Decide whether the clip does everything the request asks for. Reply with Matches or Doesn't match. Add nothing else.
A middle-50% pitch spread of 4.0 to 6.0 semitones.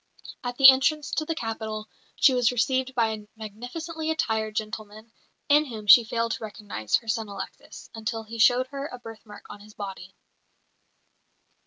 Doesn't match